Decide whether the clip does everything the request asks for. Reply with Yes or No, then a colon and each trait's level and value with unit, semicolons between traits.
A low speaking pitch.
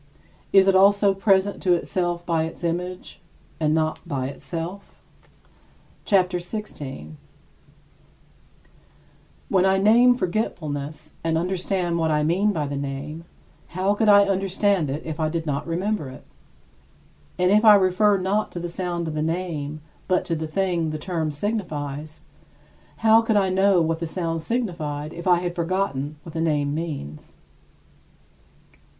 No: medium, 175 Hz